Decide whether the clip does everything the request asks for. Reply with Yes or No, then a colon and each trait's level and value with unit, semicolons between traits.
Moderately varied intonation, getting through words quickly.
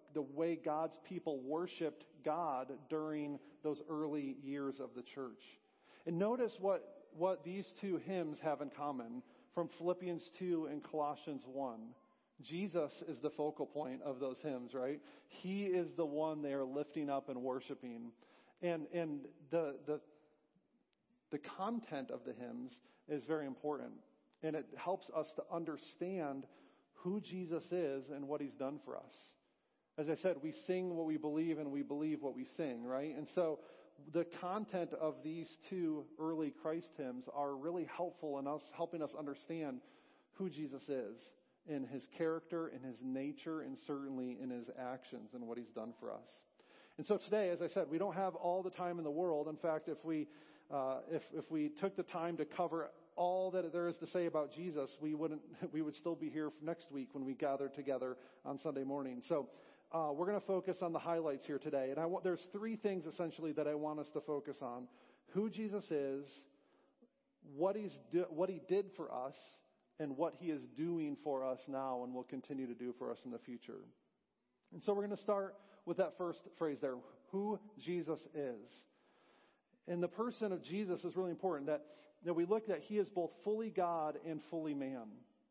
No: average, 3.7 semitones; average, 190 wpm